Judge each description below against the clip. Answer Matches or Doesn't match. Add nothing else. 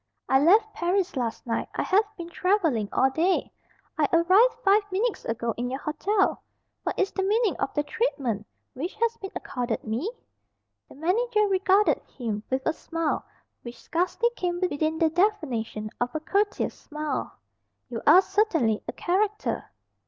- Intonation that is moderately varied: Doesn't match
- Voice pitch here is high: Matches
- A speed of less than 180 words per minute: Matches